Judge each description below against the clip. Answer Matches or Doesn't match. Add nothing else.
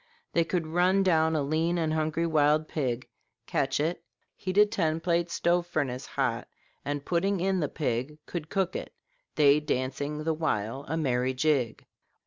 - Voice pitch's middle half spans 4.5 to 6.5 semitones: Doesn't match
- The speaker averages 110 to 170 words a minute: Matches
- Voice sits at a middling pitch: Matches